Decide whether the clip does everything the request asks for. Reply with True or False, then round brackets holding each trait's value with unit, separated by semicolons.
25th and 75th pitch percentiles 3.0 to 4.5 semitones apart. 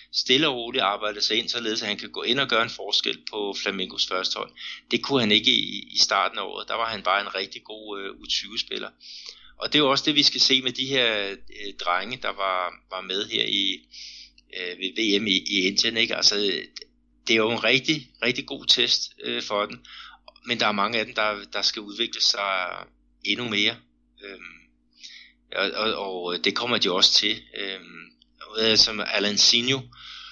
True (4.1 semitones)